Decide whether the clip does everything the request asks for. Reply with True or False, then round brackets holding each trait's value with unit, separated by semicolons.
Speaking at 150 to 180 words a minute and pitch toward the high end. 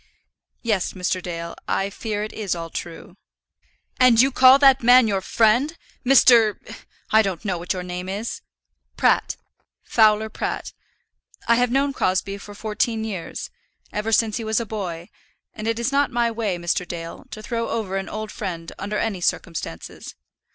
True (165 wpm; 215 Hz)